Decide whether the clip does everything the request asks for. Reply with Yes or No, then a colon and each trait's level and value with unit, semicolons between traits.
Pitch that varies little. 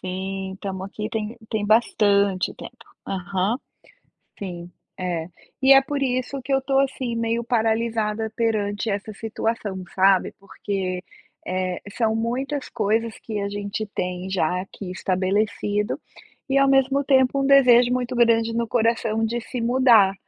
No: average, 3.6 semitones